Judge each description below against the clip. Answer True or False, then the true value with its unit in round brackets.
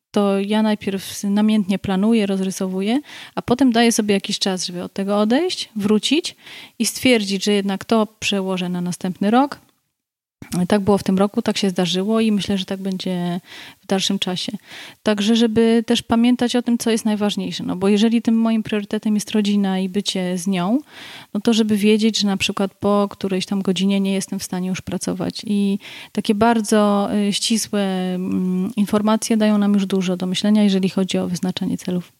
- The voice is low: False (205 Hz)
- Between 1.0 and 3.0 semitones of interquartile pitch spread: True (2.5 semitones)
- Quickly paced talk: True (180 wpm)